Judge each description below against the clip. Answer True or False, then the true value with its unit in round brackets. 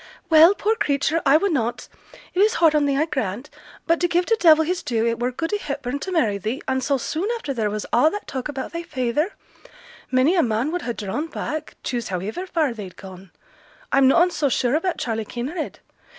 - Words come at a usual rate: False (215 wpm)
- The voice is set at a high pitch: True (285 Hz)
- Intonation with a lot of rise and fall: True (5.8 semitones)